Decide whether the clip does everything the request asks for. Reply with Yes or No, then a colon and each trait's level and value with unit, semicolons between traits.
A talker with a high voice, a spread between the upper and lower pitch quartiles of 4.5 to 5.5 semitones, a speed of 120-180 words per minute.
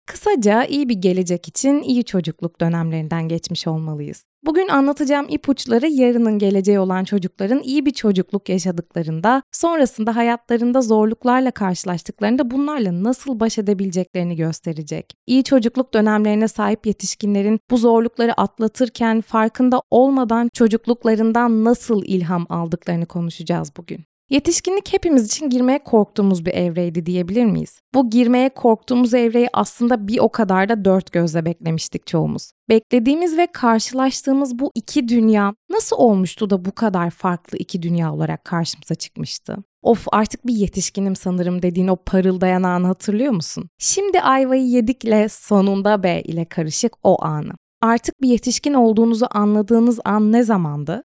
Yes: high, 220 Hz; average, 5.2 semitones; average, 135 wpm